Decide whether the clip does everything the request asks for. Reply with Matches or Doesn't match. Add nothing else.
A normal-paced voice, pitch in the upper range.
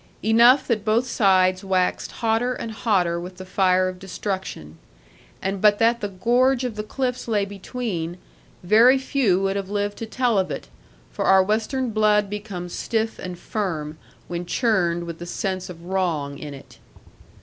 Matches